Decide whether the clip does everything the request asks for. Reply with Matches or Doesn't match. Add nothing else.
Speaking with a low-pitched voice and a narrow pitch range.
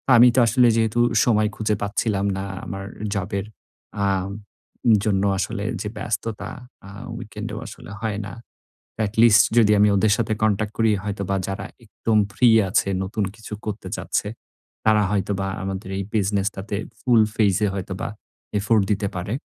Matches